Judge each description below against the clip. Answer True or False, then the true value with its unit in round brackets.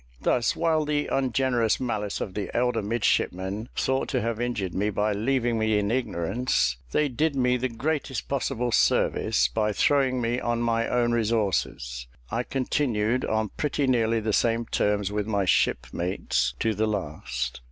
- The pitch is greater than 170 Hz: False (115 Hz)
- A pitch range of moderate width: True (3.4 semitones)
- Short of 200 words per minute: True (160 wpm)